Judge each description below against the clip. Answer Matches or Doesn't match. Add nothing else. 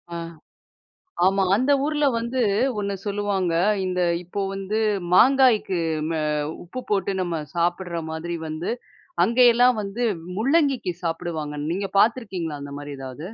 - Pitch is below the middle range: Doesn't match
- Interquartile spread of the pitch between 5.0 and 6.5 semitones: Matches